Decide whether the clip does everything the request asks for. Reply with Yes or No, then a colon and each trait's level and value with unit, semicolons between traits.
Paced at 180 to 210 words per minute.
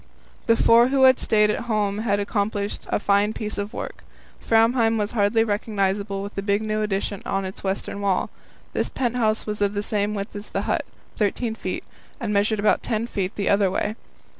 Yes: average, 200 wpm